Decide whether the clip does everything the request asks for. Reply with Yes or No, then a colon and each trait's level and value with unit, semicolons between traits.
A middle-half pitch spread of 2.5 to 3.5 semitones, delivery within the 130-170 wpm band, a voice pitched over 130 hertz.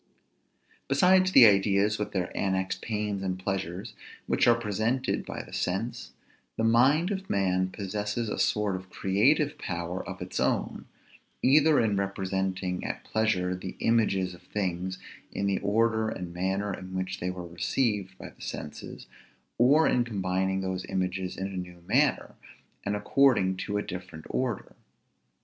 No: average, 3.2 semitones; average, 155 wpm; low, 100 Hz